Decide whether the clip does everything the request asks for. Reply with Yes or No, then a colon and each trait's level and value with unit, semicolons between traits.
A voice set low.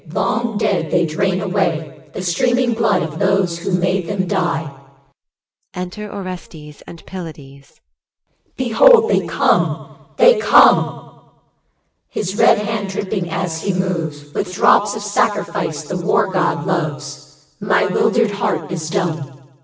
No: medium, 185 Hz